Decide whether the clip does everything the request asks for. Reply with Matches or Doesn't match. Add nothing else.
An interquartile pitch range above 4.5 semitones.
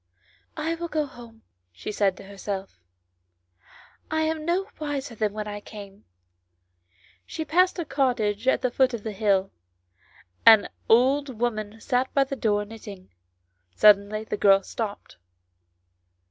Matches